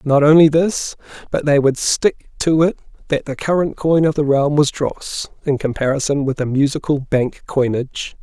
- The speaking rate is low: No, average, 180 wpm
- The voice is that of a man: Yes, male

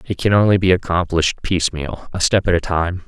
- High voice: No, very low, 90 Hz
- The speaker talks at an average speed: No, fast, 215 wpm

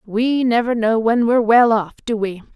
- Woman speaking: Yes, female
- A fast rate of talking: Yes, fast, 210 wpm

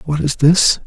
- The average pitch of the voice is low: No, medium, 155 Hz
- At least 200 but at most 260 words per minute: Yes, fast, 210 wpm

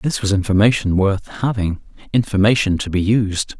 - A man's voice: Yes, male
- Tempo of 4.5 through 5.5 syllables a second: Yes, 5.0 syllables/s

